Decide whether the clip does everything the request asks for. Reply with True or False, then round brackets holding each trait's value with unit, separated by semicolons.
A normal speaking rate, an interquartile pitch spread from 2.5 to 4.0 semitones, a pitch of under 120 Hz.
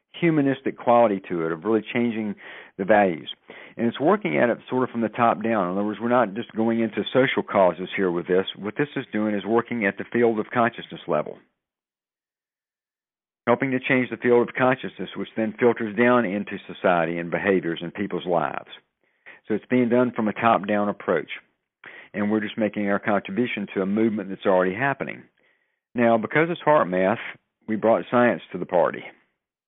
True (190 wpm; 3.3 semitones; 110 Hz)